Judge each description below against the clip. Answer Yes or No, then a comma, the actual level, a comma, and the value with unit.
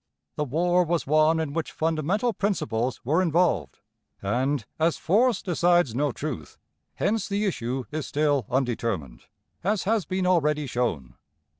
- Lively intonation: Yes, wide, 6.0 semitones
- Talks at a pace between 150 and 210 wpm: No, average, 140 wpm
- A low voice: No, medium, 155 Hz